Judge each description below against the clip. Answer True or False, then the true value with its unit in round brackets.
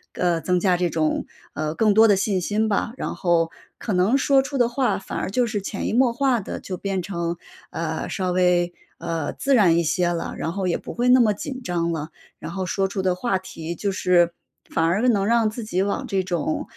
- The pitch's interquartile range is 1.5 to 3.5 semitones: False (4.1 semitones)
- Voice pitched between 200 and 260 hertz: False (190 Hz)